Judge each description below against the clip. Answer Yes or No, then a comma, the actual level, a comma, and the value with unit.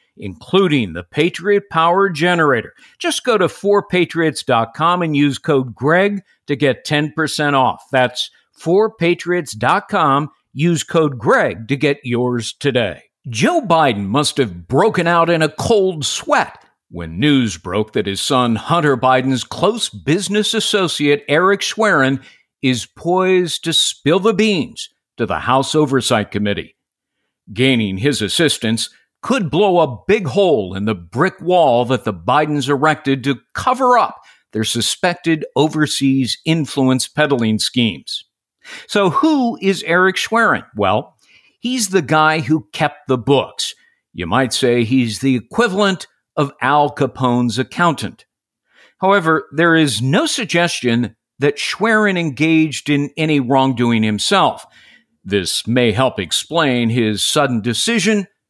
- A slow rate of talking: Yes, slow, 130 wpm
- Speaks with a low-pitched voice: No, medium, 145 Hz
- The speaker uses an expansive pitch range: Yes, wide, 6.0 semitones